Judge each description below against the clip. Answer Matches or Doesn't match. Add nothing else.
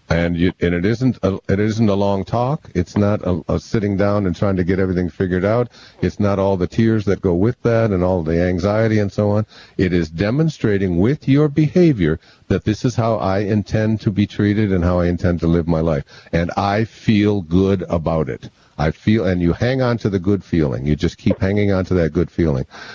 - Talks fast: Matches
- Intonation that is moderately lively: Matches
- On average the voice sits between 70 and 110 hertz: Matches